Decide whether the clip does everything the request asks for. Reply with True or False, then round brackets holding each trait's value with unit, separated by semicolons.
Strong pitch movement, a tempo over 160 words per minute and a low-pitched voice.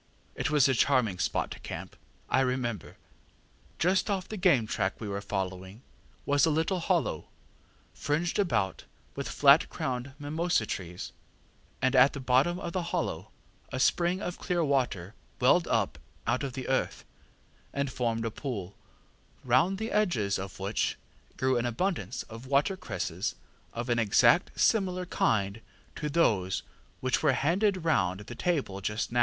False (7.7 semitones; 155 wpm; 130 Hz)